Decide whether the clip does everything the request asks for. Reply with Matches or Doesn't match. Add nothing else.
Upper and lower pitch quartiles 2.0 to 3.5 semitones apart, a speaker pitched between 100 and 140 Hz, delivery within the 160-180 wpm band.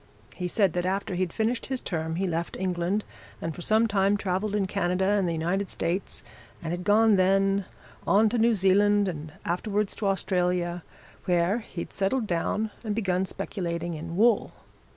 Doesn't match